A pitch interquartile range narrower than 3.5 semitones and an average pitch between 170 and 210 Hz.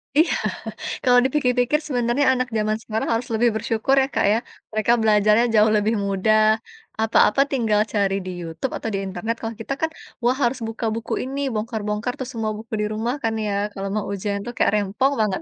No: average, 2.7 semitones; high, 225 Hz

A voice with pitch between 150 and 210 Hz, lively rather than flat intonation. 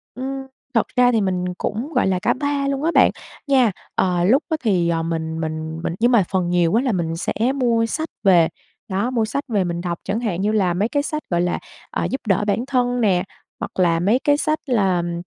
Yes: high, 205 Hz; wide, 6.2 semitones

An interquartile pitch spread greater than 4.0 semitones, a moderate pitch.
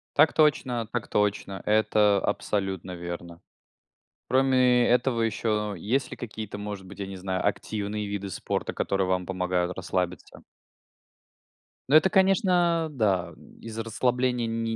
No: average, 4.5 semitones; low, 105 Hz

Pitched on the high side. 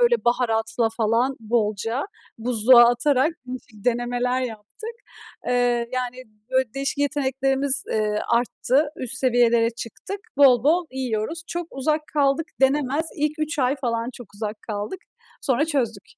Yes: very high, 250 Hz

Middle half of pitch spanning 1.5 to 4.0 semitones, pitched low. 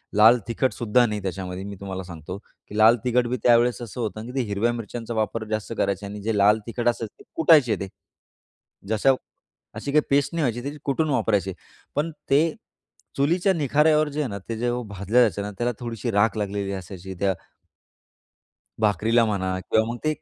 Yes: average, 3.6 semitones; low, 115 Hz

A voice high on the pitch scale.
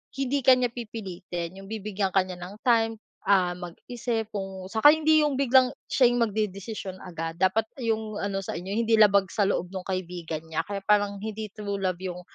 Yes: high, 200 Hz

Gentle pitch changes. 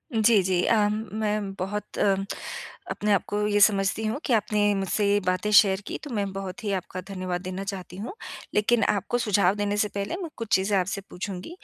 Yes: narrow, 1.7 semitones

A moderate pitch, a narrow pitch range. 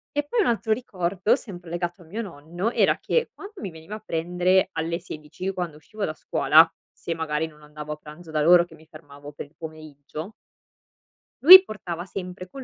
No: medium, 175 Hz; average, 4.1 semitones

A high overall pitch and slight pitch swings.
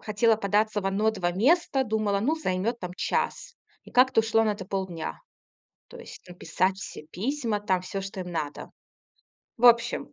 No: high, 210 Hz; average, 3.8 semitones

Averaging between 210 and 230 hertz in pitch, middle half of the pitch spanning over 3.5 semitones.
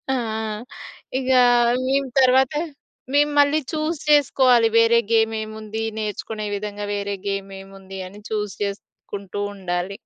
Yes: high, 220 Hz; average, 4.2 semitones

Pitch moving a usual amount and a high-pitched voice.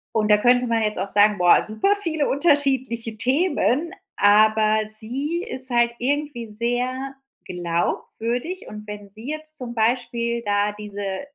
Yes: average, 4.1 semitones; high, 235 Hz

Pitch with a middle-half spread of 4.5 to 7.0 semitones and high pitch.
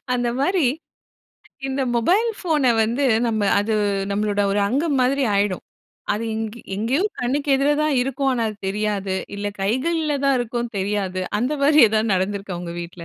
Yes: average, 5.2 semitones; high, 235 Hz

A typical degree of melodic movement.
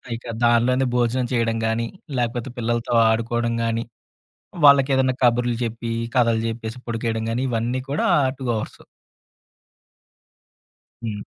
No: narrow, 1.3 semitones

